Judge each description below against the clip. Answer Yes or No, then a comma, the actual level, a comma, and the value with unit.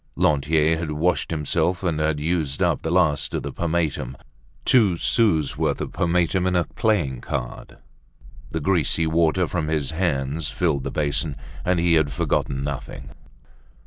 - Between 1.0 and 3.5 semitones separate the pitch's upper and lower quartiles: Yes, average, 3.1 semitones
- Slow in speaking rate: No, average, 150 wpm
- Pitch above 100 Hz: No, very low, 80 Hz